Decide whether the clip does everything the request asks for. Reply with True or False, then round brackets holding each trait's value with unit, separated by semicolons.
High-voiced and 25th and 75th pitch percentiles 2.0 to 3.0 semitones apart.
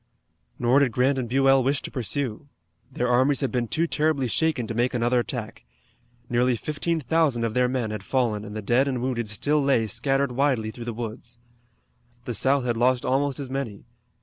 False (125 Hz; 2.7 semitones)